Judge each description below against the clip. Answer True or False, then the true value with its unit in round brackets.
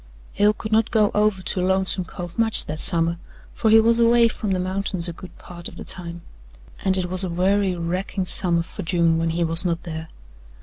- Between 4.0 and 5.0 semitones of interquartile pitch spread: False (3.2 semitones)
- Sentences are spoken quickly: True (215 wpm)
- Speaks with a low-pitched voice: False (185 Hz)